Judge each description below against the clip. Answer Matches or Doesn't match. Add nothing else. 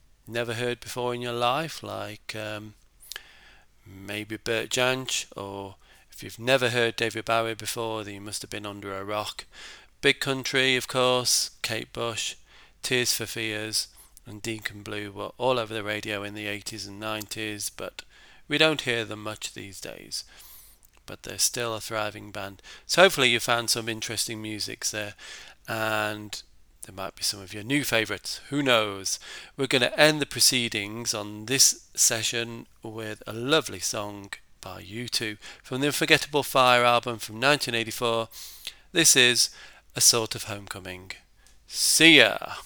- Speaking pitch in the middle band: Doesn't match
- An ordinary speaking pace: Matches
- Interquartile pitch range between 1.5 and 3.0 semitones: Matches